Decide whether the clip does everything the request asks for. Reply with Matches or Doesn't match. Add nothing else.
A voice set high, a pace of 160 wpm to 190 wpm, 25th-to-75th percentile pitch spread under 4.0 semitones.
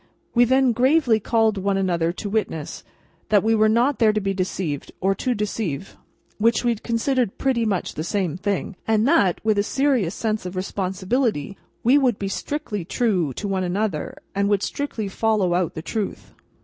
Matches